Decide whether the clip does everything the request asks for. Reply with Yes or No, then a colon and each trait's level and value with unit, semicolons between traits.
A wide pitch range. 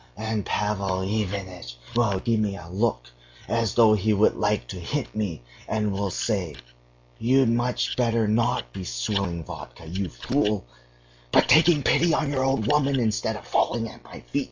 No: average, 4.0 semitones